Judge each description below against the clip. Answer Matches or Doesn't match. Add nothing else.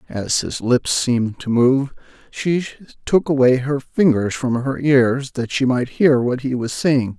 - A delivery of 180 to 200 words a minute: Matches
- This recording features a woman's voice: Doesn't match